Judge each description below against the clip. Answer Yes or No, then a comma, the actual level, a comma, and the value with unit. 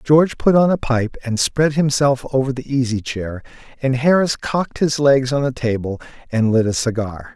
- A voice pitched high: No, low, 130 Hz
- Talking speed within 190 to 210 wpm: Yes, average, 195 wpm